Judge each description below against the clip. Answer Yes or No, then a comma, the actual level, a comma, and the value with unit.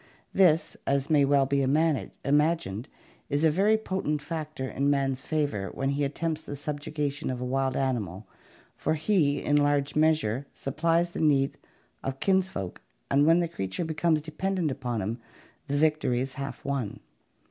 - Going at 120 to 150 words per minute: No, average, 160 wpm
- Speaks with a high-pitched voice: No, medium, 145 Hz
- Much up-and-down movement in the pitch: No, average, 2.8 semitones